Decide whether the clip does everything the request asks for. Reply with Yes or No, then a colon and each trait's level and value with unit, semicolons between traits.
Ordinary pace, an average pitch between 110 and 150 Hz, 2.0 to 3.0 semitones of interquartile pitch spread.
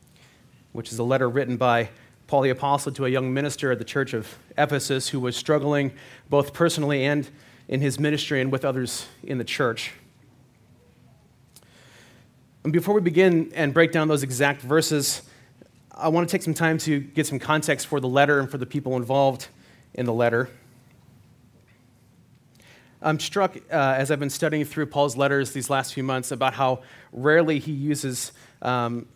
Yes: average, 175 wpm; low, 135 Hz; narrow, 2.6 semitones